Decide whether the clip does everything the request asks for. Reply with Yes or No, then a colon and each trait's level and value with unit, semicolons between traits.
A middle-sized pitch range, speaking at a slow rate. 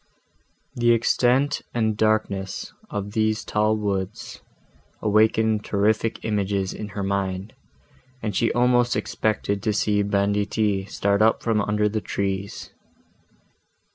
No: narrow, 1.7 semitones; slow, 115 wpm